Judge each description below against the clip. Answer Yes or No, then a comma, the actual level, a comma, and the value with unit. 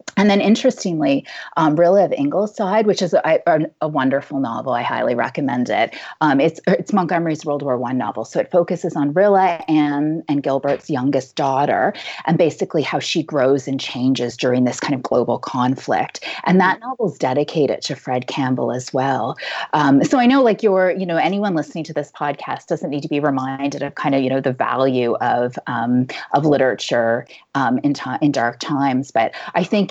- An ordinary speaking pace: Yes, average, 195 wpm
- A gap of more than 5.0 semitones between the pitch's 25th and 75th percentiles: Yes, wide, 5.6 semitones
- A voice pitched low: No, medium, 145 Hz